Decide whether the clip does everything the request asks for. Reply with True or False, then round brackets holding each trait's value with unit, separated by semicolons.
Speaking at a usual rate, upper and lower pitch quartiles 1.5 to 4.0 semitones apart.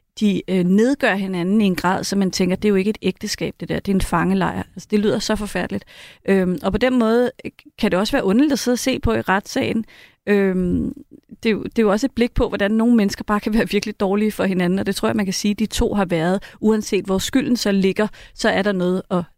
False (260 wpm; 3.1 semitones)